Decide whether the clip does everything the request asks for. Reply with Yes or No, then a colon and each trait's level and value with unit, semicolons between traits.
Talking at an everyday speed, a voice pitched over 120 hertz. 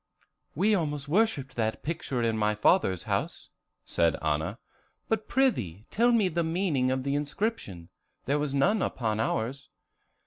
Yes: average, 150 wpm; medium, 140 Hz